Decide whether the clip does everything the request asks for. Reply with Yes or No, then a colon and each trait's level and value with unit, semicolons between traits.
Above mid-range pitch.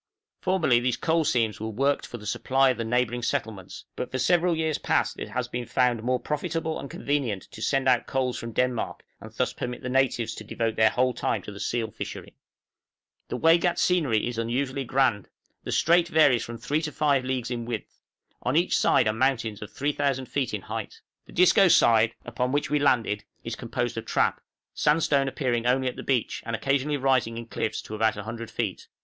No: low, 125 Hz